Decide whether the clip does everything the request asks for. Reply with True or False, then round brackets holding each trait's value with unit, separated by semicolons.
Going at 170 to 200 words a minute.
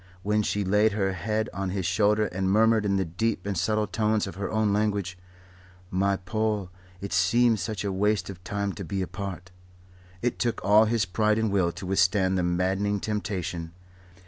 True (185 wpm)